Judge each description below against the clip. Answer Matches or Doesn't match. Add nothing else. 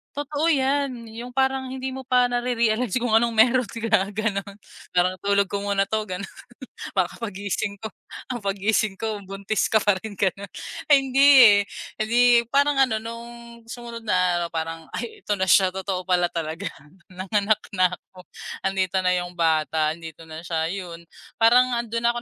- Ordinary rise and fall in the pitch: Matches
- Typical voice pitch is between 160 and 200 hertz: Doesn't match